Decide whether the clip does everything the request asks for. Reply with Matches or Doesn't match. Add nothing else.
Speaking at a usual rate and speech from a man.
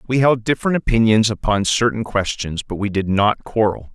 Matches